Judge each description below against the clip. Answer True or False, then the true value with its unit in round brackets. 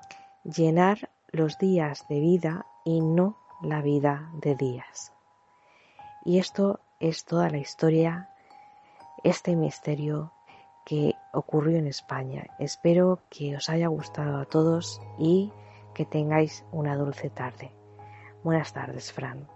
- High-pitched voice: False (155 Hz)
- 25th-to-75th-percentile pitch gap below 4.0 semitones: True (3.1 semitones)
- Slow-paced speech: True (120 wpm)